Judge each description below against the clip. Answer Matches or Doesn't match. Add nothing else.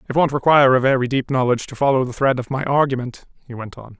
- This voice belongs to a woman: Doesn't match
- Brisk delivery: Matches